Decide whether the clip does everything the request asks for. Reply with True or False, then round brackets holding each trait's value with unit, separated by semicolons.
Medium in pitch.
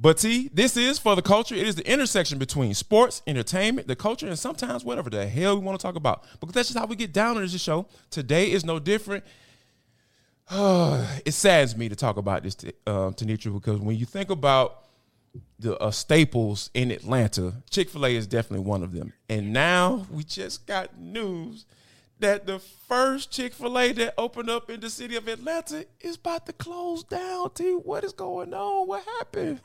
True (180 Hz)